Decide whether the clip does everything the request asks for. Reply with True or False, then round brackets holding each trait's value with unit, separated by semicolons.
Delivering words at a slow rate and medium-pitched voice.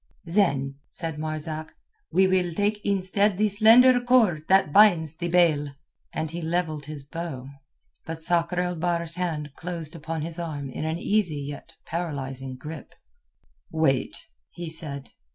False (145 wpm; 165 Hz)